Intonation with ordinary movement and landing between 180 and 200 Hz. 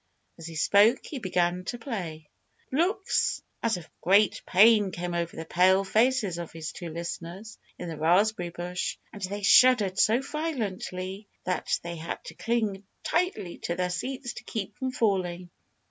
Yes: average, 4.6 semitones; high, 190 Hz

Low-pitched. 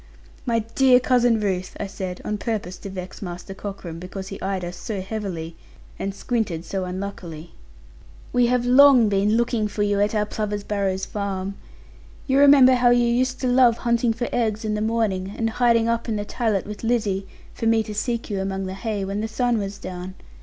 No: high, 210 Hz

